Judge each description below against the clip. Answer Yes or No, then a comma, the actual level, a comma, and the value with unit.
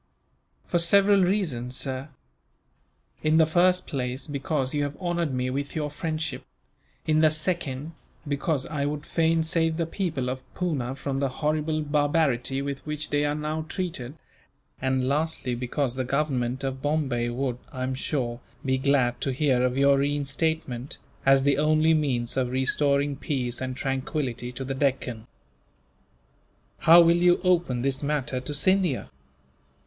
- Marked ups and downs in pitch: No, average, 3.3 semitones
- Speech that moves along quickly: No, average, 155 wpm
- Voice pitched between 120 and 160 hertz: Yes, medium, 140 Hz